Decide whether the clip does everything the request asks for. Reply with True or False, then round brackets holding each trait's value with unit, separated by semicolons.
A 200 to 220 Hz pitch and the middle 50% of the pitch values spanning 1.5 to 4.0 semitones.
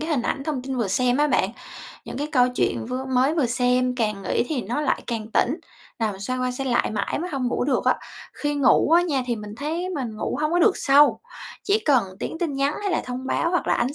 False (265 Hz; 3.4 semitones)